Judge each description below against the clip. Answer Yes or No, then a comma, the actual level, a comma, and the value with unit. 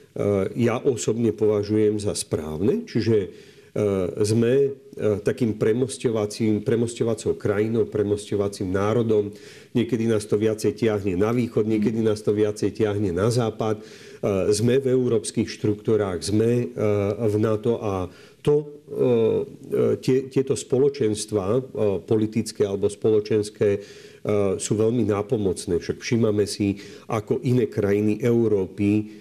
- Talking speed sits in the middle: No, slow, 105 wpm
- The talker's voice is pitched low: Yes, low, 105 Hz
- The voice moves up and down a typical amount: No, narrow, 1.9 semitones